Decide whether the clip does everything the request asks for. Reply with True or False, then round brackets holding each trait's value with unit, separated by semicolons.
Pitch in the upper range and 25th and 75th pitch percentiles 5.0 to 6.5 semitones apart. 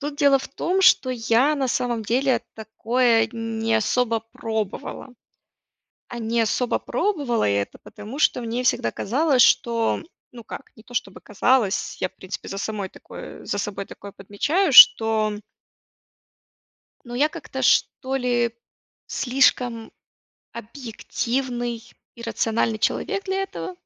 False (235 Hz; 2.9 semitones)